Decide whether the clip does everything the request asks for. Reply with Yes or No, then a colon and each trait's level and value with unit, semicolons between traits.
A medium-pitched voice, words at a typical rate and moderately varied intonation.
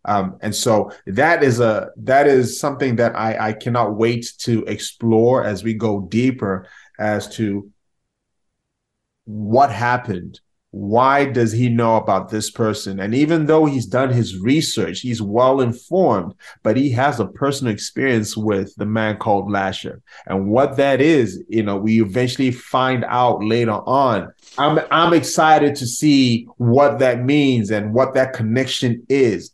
No: low, 120 Hz; average, 155 wpm; average, 3.6 semitones